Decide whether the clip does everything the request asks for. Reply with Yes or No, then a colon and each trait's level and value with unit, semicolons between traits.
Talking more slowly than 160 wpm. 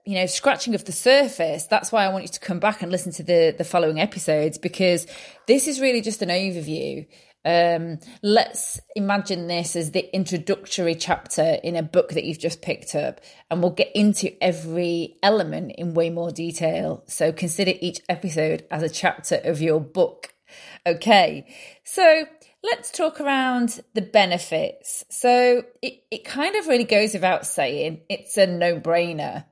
No: average, 170 wpm